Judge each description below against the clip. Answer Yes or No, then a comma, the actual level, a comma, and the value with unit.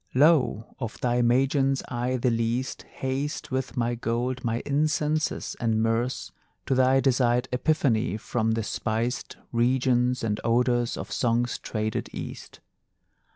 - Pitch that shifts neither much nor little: No, narrow, 2.2 semitones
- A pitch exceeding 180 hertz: No, low, 125 Hz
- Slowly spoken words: Yes, slow, 130 wpm